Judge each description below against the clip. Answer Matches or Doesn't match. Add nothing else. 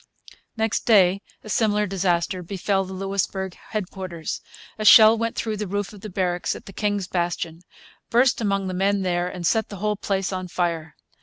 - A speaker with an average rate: Matches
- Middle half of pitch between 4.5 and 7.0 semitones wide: Doesn't match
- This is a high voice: Matches